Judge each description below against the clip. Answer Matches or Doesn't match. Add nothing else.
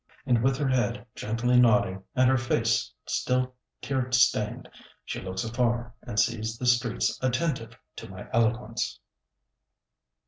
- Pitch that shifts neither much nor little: Doesn't match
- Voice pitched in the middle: Doesn't match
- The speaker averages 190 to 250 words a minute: Doesn't match